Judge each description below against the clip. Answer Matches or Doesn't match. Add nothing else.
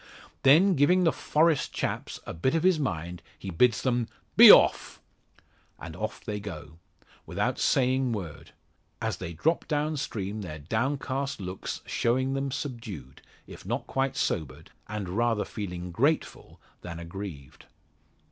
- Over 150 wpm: Doesn't match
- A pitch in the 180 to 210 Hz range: Doesn't match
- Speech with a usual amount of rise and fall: Doesn't match